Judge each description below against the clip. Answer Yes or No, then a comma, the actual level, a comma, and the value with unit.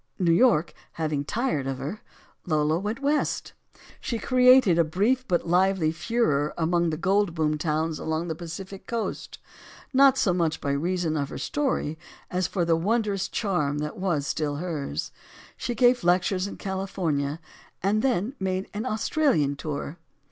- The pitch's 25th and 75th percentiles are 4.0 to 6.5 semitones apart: Yes, average, 5.2 semitones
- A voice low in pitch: No, medium, 175 Hz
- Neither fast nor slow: Yes, average, 155 wpm